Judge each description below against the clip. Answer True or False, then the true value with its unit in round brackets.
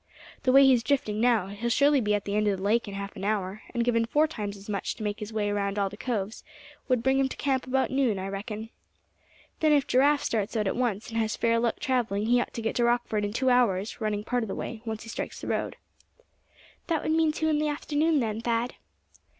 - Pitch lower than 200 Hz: False (230 Hz)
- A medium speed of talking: False (250 wpm)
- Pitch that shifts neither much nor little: True (3.8 semitones)